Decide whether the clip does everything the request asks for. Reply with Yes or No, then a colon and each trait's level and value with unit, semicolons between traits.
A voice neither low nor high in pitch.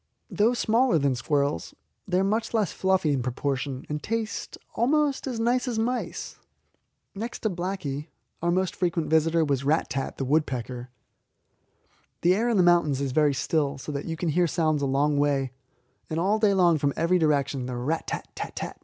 Yes: medium, 160 Hz